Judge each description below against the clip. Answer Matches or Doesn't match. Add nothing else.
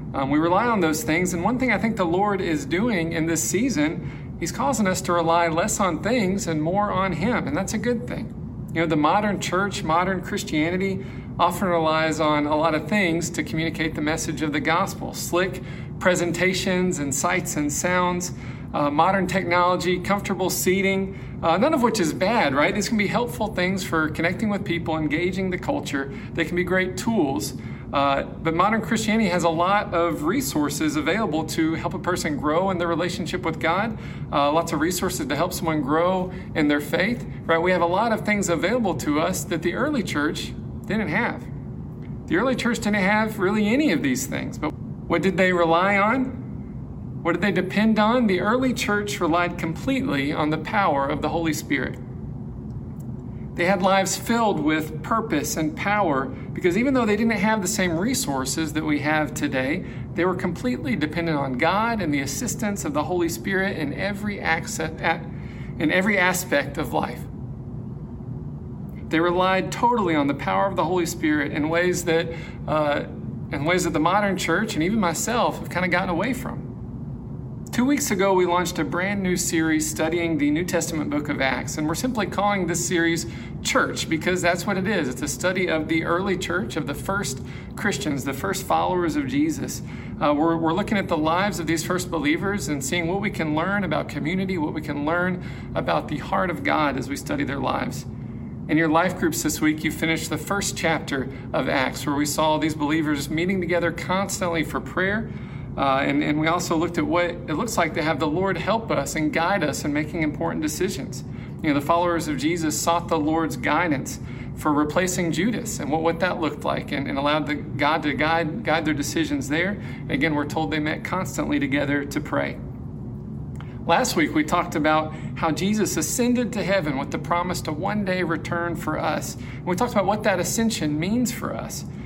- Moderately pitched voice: Matches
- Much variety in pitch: Doesn't match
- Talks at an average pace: Matches